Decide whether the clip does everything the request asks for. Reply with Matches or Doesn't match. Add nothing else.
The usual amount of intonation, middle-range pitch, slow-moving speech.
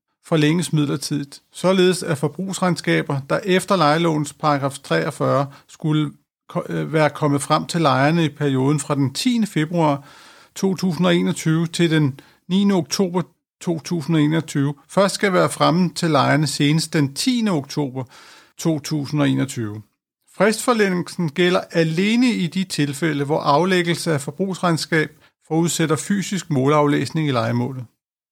Matches